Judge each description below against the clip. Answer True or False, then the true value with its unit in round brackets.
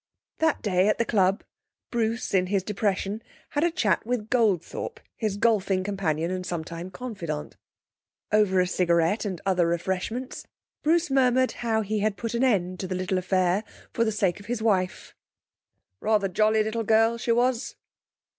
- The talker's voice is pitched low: False (210 Hz)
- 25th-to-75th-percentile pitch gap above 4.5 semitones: False (3.8 semitones)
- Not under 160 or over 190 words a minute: True (165 wpm)